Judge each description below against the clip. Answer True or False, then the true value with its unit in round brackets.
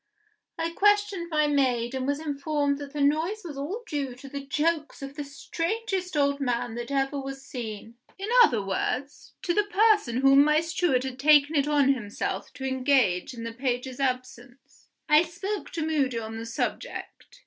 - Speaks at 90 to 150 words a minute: False (180 wpm)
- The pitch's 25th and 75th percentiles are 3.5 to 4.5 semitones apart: True (3.9 semitones)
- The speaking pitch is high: True (280 Hz)